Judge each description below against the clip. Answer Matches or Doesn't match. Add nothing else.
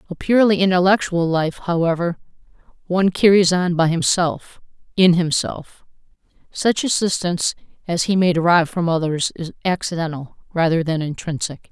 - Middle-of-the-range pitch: Matches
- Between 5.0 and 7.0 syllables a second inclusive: Matches